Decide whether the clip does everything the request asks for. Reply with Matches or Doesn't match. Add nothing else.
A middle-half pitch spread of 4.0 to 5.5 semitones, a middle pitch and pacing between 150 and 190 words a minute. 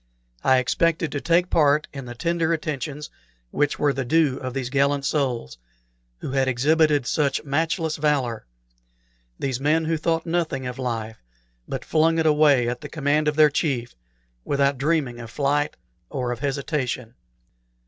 Doesn't match